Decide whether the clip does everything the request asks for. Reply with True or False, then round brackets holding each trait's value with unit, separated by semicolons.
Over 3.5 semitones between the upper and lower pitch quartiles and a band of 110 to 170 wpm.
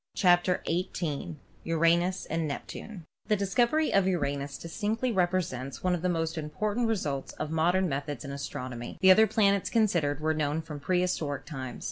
True (4.5 semitones; 165 wpm)